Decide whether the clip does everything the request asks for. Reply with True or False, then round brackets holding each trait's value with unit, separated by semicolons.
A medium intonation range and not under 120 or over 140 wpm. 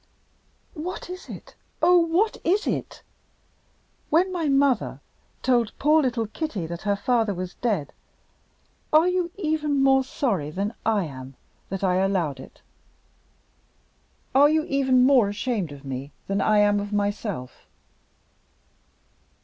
False (7.7 semitones; 135 wpm)